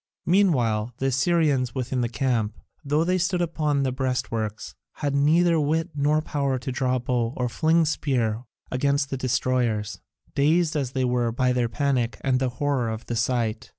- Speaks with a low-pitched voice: Yes, low, 130 Hz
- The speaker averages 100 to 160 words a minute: No, average, 170 wpm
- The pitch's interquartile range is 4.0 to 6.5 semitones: No, average, 3.4 semitones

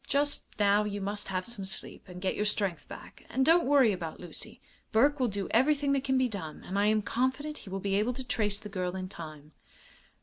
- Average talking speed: No, fast, 230 wpm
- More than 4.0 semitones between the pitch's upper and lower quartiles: Yes, wide, 5.4 semitones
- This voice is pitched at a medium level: No, high, 210 Hz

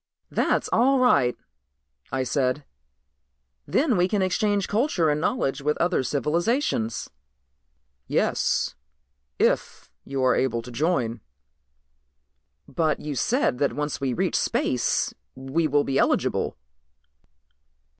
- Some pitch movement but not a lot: No, wide, 6.1 semitones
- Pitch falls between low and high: Yes, medium, 150 Hz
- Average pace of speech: No, slow, 115 wpm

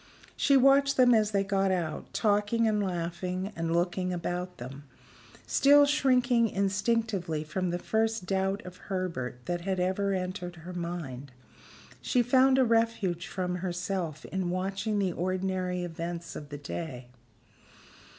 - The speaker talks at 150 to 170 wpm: No, average, 140 wpm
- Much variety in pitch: No, average, 3.4 semitones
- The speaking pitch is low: No, medium, 185 Hz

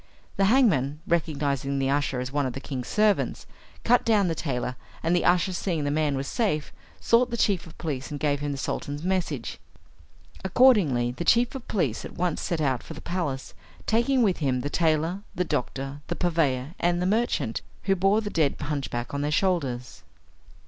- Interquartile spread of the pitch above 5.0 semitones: Yes, wide, 5.5 semitones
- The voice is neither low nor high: Yes, medium, 155 Hz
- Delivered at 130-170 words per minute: No, average, 190 wpm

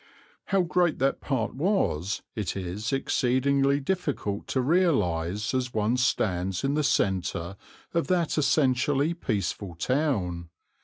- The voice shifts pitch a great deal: Yes, wide, 7.1 semitones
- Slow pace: Yes, slow, 120 wpm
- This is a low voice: Yes, low, 130 Hz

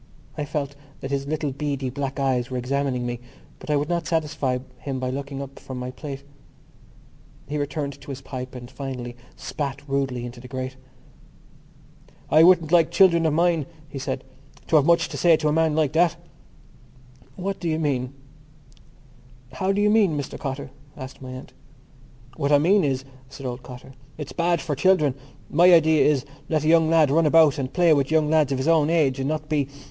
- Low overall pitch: No, medium, 145 Hz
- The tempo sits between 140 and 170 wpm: No, average, 190 wpm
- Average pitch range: Yes, average, 3.1 semitones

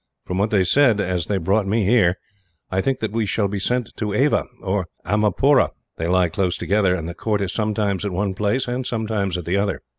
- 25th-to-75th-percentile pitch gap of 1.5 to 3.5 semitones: Yes, average, 2.9 semitones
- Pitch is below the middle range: Yes, low, 100 Hz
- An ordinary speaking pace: No, fast, 220 wpm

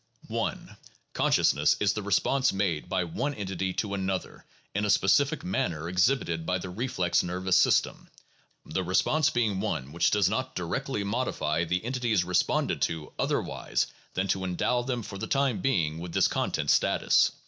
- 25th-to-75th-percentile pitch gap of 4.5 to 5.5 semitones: Yes, average, 5.1 semitones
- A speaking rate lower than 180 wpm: Yes, average, 170 wpm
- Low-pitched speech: Yes, very low, 95 Hz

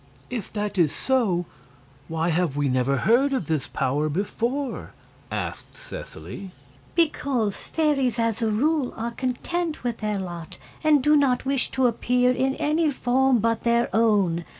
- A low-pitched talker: No, high, 235 Hz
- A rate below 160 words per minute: Yes, average, 150 wpm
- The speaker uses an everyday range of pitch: No, wide, 5.9 semitones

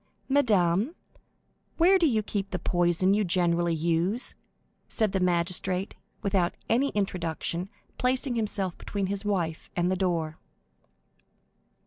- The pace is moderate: No, slow, 120 wpm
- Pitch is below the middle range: No, high, 190 Hz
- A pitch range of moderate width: Yes, average, 3.6 semitones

